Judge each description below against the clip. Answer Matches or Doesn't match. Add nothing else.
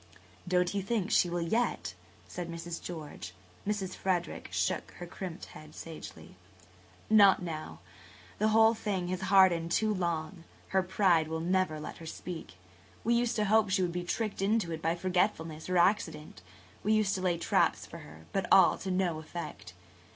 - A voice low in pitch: Doesn't match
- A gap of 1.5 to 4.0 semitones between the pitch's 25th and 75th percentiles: Matches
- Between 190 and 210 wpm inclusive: Doesn't match